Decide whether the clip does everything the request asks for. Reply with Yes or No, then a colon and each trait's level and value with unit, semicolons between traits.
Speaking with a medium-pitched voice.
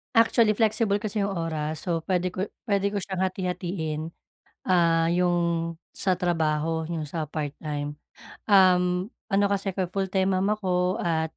Yes: medium, 180 Hz